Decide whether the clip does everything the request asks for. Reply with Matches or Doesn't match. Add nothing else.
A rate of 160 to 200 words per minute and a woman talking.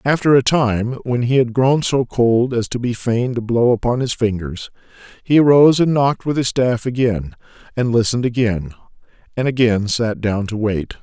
Doesn't match